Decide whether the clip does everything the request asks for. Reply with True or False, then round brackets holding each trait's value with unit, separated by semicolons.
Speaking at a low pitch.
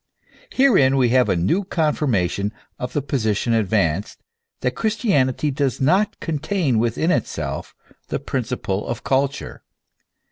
True (130 Hz)